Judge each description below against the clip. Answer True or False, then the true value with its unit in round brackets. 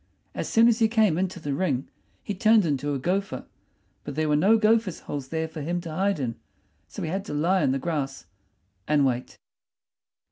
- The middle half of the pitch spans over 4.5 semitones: True (5.3 semitones)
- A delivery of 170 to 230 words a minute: True (205 wpm)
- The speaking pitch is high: False (165 Hz)